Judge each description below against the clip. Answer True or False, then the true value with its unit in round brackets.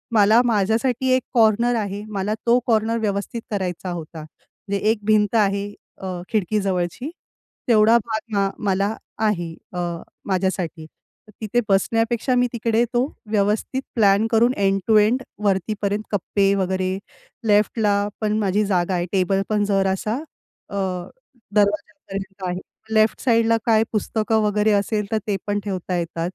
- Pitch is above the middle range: True (210 Hz)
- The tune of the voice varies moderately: False (2.3 semitones)